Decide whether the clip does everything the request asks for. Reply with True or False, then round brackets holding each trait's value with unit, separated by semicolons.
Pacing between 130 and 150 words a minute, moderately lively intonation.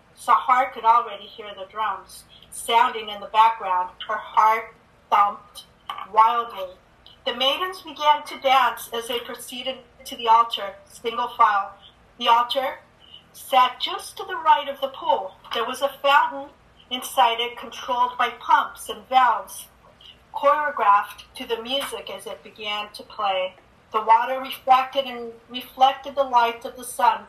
True (145 wpm; 3.5 semitones)